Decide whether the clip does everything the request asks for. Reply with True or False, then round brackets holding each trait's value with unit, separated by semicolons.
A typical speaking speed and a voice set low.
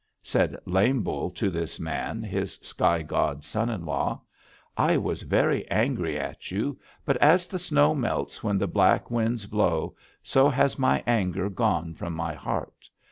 True (165 wpm; 100 Hz)